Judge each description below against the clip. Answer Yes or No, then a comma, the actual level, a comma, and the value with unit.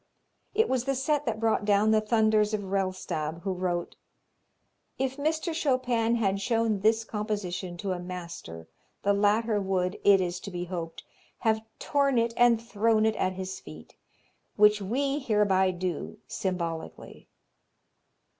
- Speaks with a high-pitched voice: Yes, high, 210 Hz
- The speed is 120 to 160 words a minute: Yes, average, 145 wpm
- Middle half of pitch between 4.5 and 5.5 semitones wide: No, average, 3.7 semitones